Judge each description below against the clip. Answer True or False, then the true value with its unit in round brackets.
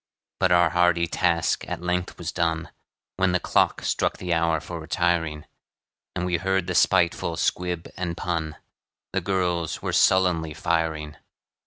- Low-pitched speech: True (85 Hz)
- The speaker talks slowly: False (150 wpm)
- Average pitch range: False (1.6 semitones)